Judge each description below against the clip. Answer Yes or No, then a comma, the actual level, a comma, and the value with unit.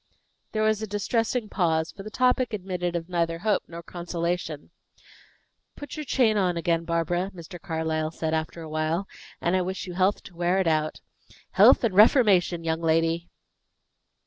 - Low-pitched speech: No, medium, 175 Hz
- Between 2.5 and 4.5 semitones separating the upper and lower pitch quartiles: Yes, average, 3.6 semitones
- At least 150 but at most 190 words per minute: Yes, average, 170 wpm